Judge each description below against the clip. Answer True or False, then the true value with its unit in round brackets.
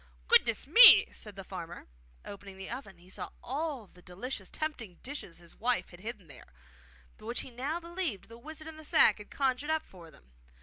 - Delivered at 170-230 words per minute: True (205 wpm)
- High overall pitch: True (230 Hz)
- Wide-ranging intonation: True (7.9 semitones)